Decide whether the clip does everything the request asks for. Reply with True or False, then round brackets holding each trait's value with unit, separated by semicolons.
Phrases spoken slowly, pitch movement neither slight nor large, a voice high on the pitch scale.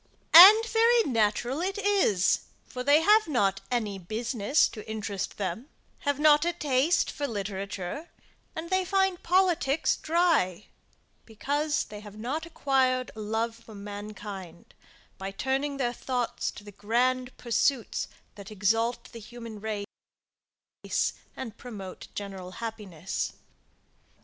False (125 wpm; 6.3 semitones; 240 Hz)